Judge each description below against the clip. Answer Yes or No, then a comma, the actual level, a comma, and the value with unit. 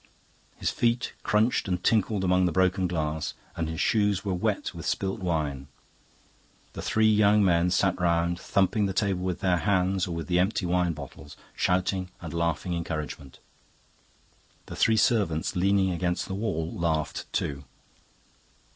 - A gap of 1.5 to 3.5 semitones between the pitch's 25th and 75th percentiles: Yes, average, 2.8 semitones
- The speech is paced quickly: No, average, 155 wpm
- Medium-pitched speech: No, very low, 90 Hz